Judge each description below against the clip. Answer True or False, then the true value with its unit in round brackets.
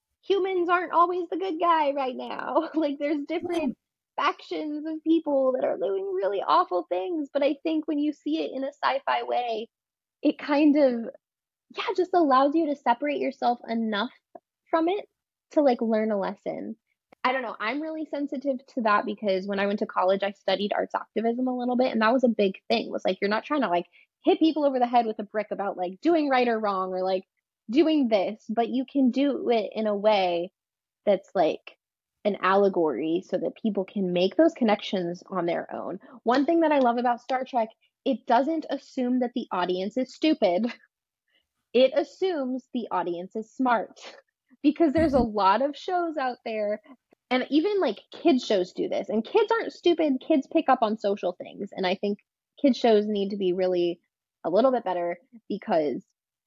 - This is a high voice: True (250 Hz)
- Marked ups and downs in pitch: True (6.6 semitones)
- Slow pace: False (200 wpm)